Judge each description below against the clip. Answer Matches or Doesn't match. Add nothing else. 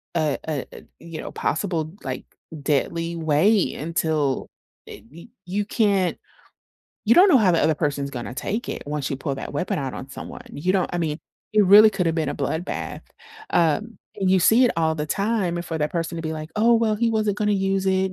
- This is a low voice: Doesn't match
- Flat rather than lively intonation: Doesn't match